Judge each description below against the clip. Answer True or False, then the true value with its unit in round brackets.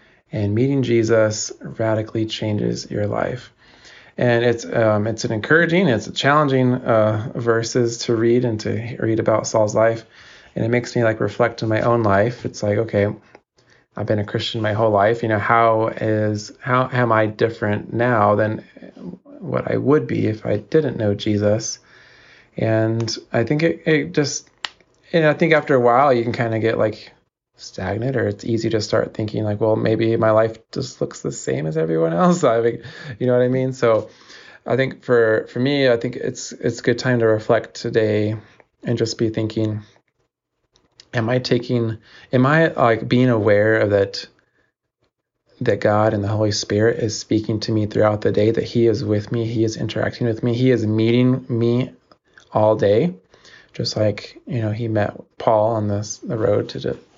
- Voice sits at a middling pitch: False (115 Hz)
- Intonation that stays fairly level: True (2.2 semitones)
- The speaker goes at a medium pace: True (190 wpm)